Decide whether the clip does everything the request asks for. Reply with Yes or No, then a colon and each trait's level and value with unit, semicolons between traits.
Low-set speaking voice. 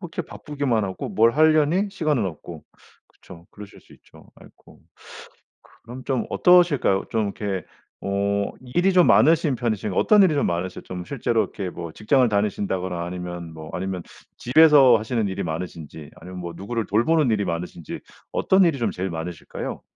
Yes: low, 105 Hz